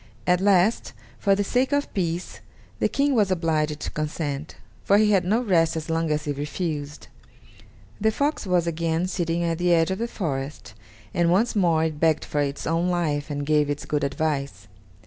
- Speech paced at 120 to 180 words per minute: No, average, 190 wpm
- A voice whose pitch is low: No, medium, 165 Hz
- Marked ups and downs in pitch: No, average, 3.9 semitones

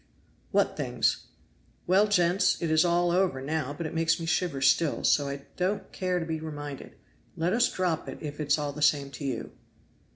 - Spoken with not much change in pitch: No, average, 3.4 semitones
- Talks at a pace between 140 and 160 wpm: No, average, 200 wpm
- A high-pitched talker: No, medium, 160 Hz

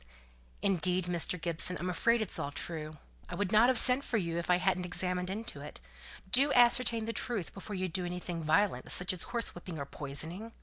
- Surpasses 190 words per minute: Yes, average, 200 wpm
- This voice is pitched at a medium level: Yes, medium, 180 Hz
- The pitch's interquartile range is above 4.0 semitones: Yes, average, 4.4 semitones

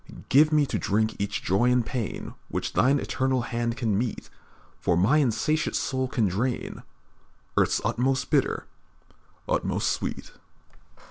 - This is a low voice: Yes, low, 125 Hz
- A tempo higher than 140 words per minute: No, slow, 135 wpm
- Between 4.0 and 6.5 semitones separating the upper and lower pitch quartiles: No, average, 3.3 semitones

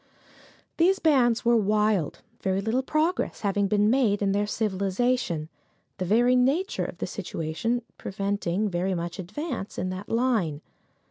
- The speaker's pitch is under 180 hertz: No, high, 210 Hz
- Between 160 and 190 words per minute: No, average, 140 wpm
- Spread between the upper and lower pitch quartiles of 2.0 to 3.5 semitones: No, average, 4.5 semitones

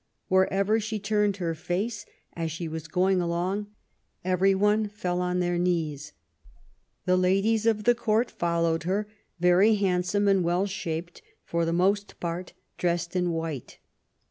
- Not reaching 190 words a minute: Yes, average, 145 wpm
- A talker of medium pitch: Yes, medium, 180 Hz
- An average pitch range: Yes, average, 3.1 semitones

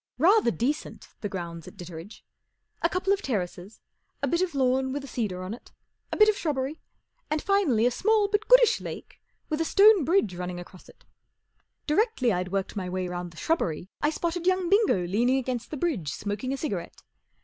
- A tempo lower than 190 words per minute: No, average, 195 wpm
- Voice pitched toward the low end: No, very high, 260 Hz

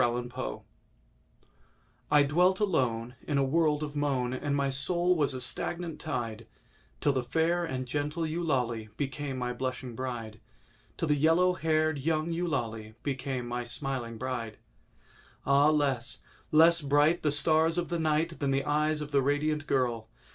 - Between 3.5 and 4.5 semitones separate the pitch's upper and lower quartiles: Yes, average, 3.8 semitones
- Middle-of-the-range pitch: Yes, medium, 145 Hz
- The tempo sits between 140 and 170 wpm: Yes, average, 150 wpm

